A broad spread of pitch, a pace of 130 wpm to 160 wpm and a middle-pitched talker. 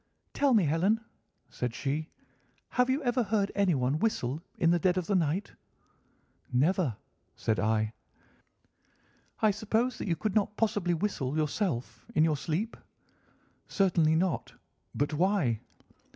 Yes: wide, 6.0 semitones; slow, 135 wpm; medium, 175 Hz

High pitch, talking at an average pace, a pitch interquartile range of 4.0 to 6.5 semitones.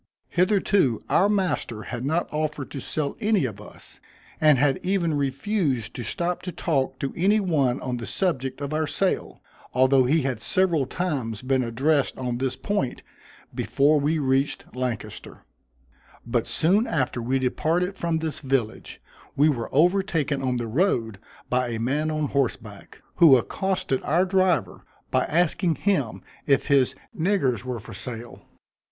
No: medium, 140 Hz; average, 155 wpm; average, 5.2 semitones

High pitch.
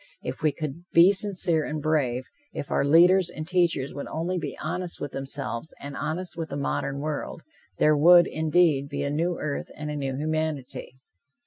No: medium, 155 Hz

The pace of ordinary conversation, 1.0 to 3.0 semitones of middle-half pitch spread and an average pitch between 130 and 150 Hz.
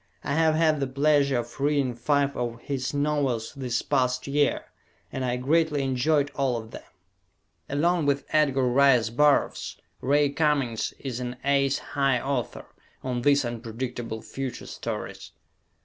Yes: average, 145 wpm; narrow, 2.6 semitones; low, 135 Hz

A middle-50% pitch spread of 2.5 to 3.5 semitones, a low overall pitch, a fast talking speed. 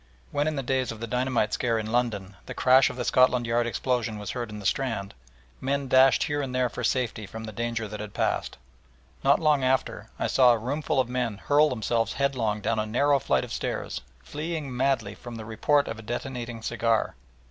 Yes: average, 3.0 semitones; low, 120 Hz; fast, 210 wpm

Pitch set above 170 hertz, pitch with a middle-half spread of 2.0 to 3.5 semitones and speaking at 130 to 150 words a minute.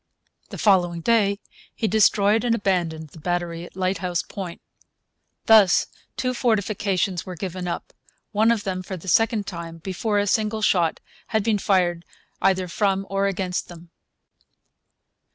Yes: high, 190 Hz; average, 3.1 semitones; average, 145 wpm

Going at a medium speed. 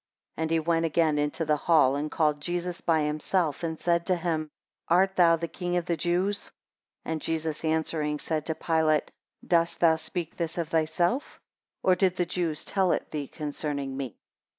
Yes: average, 190 wpm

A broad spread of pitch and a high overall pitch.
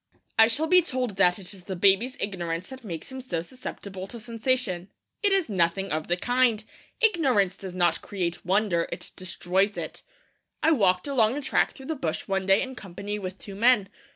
Yes: wide, 5.7 semitones; high, 200 Hz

